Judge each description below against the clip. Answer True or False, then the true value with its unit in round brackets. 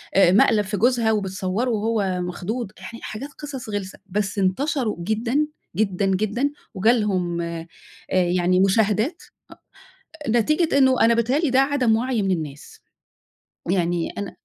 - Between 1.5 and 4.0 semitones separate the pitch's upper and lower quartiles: False (4.5 semitones)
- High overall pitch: True (210 Hz)